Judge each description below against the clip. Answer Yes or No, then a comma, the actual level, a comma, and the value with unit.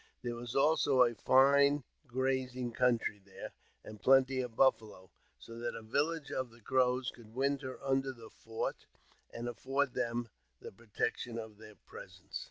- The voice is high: No, low, 125 Hz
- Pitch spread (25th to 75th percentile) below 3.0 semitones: Yes, narrow, 2.6 semitones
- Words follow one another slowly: No, average, 160 wpm